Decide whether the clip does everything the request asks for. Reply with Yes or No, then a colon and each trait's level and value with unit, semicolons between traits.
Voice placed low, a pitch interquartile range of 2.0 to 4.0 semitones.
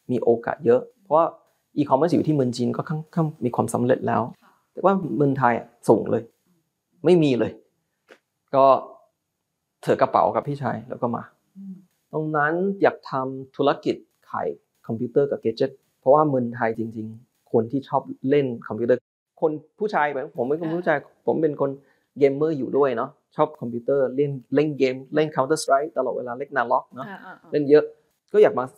No: medium, 145 Hz; average, 3.5 semitones